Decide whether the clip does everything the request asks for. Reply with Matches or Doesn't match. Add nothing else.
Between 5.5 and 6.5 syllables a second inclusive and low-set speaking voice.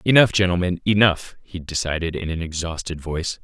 Matches